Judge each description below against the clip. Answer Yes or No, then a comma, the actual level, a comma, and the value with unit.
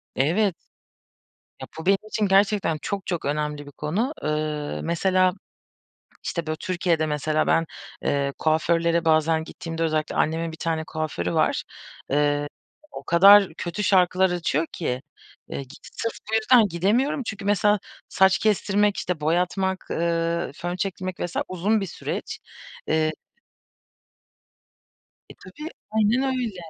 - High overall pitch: No, medium, 170 Hz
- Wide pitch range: No, average, 4.0 semitones